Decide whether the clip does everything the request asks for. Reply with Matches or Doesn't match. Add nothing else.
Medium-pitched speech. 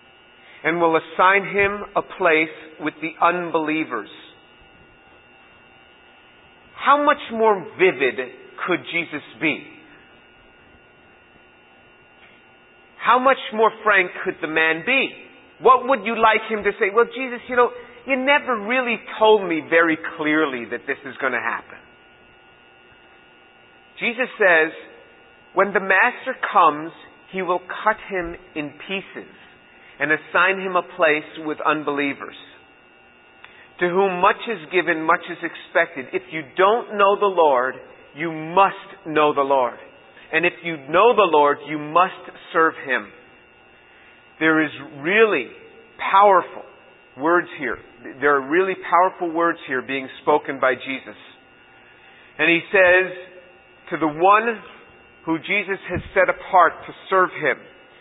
Matches